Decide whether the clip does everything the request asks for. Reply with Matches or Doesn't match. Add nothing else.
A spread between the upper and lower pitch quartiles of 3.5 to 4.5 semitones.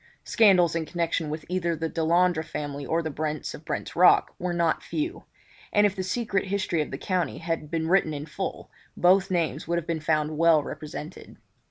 Doesn't match